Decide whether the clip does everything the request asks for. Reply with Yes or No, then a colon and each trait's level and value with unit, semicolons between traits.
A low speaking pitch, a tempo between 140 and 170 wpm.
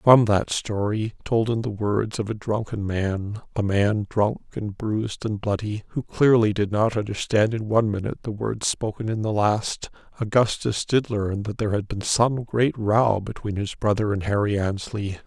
No: low, 105 Hz; average, 180 wpm